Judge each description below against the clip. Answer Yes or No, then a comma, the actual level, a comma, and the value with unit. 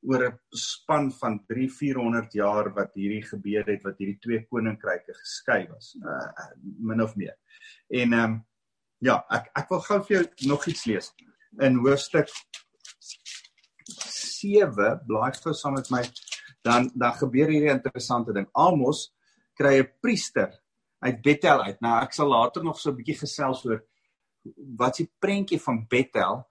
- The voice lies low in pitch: Yes, low, 130 Hz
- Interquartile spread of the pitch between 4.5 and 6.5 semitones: Yes, average, 4.8 semitones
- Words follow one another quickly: No, average, 160 wpm